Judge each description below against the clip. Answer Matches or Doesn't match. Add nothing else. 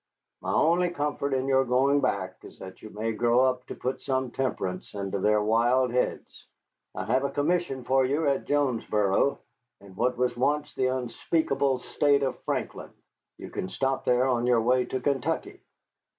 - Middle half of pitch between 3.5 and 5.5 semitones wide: Doesn't match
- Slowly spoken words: Doesn't match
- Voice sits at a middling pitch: Doesn't match